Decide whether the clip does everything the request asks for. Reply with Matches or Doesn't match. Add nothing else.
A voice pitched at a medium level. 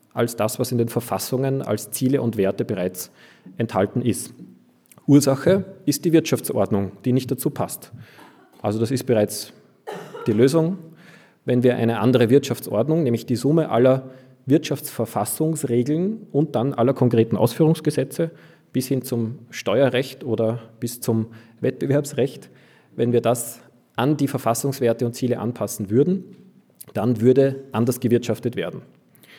Doesn't match